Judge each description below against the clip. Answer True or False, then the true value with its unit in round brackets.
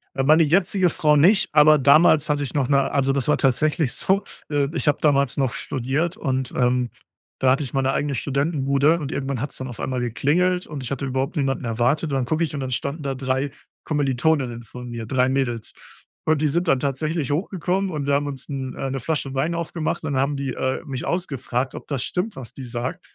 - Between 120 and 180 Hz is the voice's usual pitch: True (140 Hz)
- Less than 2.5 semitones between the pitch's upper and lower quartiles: False (2.8 semitones)